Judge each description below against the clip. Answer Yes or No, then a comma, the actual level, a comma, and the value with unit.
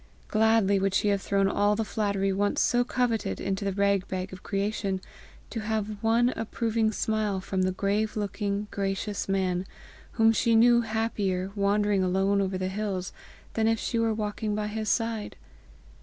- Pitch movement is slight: Yes, narrow, 2.2 semitones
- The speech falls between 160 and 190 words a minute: Yes, average, 170 wpm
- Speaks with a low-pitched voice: No, high, 205 Hz